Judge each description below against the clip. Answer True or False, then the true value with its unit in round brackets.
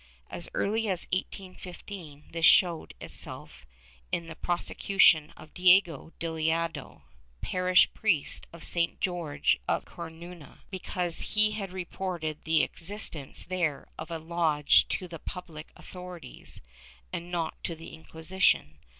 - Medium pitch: True (170 Hz)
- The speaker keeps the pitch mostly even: True (2.3 semitones)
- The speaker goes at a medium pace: False (125 wpm)